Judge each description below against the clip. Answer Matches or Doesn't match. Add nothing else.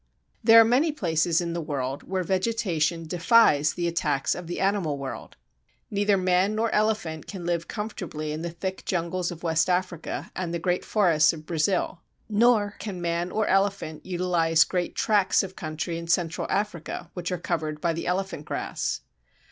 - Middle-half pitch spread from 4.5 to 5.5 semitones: Doesn't match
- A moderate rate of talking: Matches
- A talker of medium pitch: Matches